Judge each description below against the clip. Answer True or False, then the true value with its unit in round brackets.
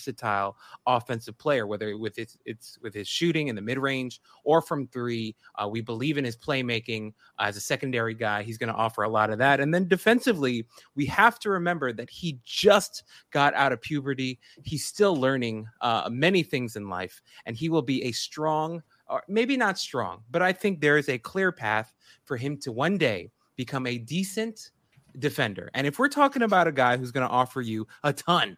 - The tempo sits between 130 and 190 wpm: False (205 wpm)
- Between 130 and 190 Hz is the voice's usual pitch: True (135 Hz)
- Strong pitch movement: True (6.3 semitones)